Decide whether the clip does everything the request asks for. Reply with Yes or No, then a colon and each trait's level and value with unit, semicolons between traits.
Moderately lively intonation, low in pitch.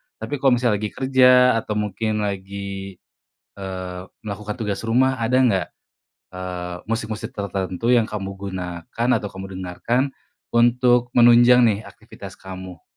Yes: average, 4.2 semitones; low, 105 Hz